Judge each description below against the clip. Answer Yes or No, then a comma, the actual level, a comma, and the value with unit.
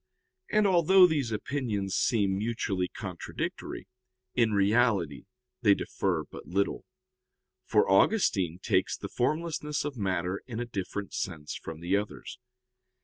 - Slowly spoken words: Yes, slow, 125 wpm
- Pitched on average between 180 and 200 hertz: No, low, 105 Hz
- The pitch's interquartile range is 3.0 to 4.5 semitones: No, average, 5.2 semitones